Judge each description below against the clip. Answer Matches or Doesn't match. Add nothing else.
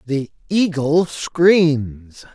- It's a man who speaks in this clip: Matches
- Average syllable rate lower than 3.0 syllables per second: Matches